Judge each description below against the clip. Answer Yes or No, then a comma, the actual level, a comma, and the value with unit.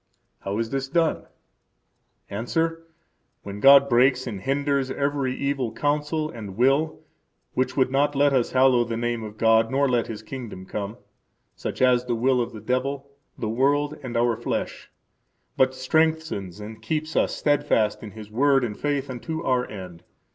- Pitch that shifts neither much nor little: Yes, average, 3.8 semitones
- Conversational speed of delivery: Yes, average, 170 wpm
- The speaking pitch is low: Yes, low, 130 Hz